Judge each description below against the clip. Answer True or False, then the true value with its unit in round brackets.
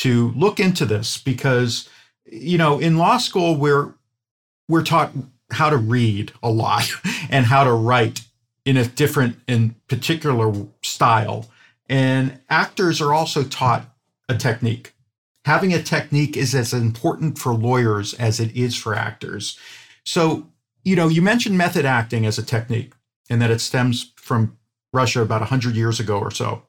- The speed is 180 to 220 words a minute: False (155 wpm)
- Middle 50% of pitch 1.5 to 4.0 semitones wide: False (4.4 semitones)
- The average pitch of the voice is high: False (125 Hz)